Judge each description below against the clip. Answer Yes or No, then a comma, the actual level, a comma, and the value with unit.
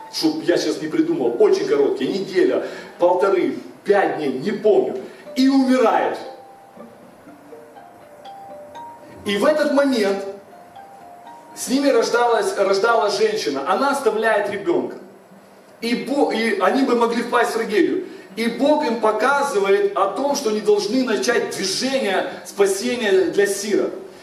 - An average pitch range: No, wide, 7.0 semitones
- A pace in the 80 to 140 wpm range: Yes, average, 125 wpm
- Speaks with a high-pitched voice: Yes, high, 245 Hz